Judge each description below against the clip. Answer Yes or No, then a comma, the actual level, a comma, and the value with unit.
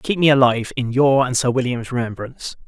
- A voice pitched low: Yes, low, 125 Hz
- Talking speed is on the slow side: No, average, 200 wpm